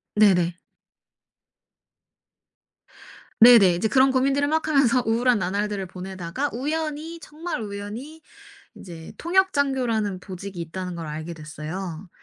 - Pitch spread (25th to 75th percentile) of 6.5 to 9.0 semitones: Yes, wide, 7.2 semitones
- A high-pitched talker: Yes, high, 210 Hz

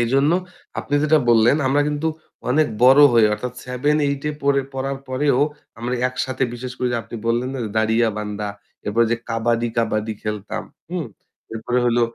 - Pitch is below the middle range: Yes, low, 125 Hz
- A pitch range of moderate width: Yes, average, 3.3 semitones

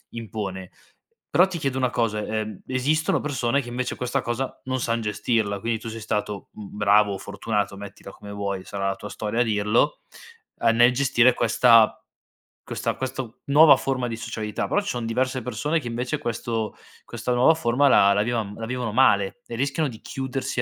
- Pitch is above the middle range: No, low, 115 Hz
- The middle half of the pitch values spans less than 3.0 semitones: No, average, 3.6 semitones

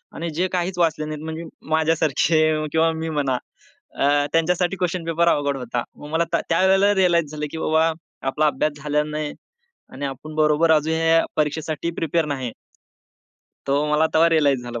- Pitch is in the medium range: Yes, medium, 160 Hz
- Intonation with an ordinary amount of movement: No, narrow, 1.9 semitones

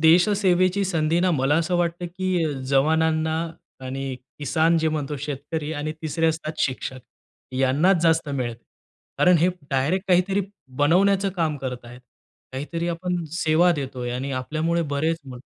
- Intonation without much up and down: No, average, 4.0 semitones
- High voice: No, medium, 160 Hz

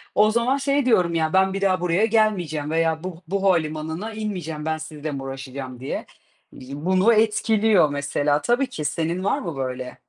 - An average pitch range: No, wide, 5.8 semitones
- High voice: No, medium, 170 Hz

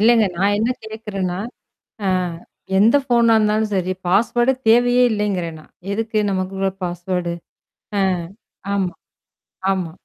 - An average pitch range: Yes, average, 3.3 semitones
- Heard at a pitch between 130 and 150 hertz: No, high, 205 Hz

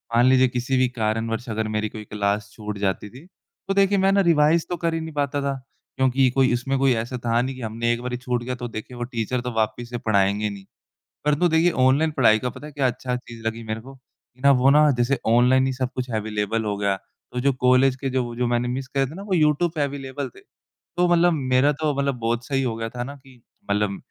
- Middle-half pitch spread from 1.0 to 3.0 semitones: No, average, 3.6 semitones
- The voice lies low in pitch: Yes, low, 125 Hz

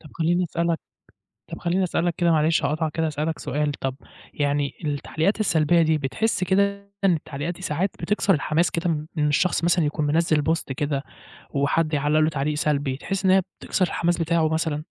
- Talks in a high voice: No, medium, 160 Hz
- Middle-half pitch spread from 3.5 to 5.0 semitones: No, average, 2.7 semitones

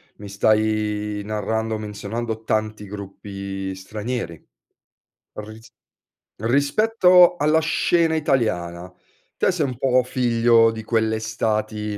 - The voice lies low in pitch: Yes, low, 110 Hz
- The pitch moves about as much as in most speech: Yes, average, 3.1 semitones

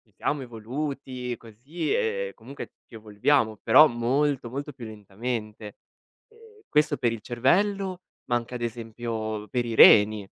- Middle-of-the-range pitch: No, low, 120 Hz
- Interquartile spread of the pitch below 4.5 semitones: No, average, 4.9 semitones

